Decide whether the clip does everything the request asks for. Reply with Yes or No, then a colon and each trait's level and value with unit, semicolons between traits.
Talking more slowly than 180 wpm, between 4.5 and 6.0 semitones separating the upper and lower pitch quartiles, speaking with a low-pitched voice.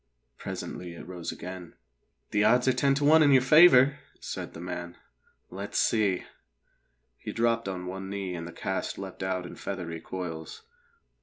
Yes: average, 165 wpm; wide, 5.6 semitones; very low, 95 Hz